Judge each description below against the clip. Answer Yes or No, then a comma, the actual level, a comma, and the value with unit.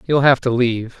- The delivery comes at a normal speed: No, fast, 240 wpm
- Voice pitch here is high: No, low, 125 Hz